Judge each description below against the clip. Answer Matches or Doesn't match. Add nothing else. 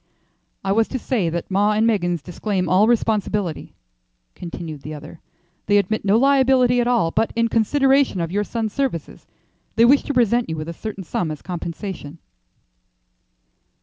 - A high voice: Matches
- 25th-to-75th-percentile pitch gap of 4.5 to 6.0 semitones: Matches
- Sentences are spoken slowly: Doesn't match